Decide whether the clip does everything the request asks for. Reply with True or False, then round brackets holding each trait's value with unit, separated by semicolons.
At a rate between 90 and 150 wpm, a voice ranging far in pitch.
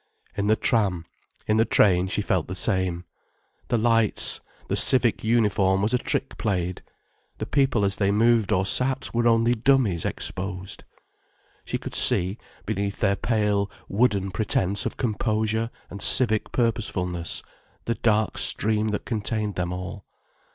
False (145 wpm; 3.2 semitones)